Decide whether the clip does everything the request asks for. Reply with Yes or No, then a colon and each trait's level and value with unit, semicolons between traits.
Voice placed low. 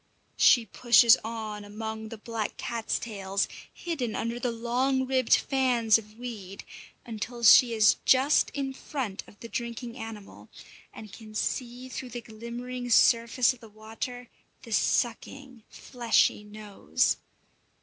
No: high, 230 Hz